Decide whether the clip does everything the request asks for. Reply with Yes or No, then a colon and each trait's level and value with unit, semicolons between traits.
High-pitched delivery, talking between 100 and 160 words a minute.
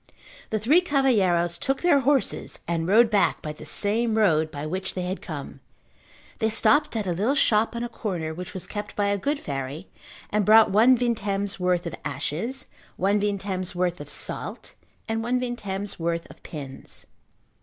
No: high, 200 Hz; average, 175 wpm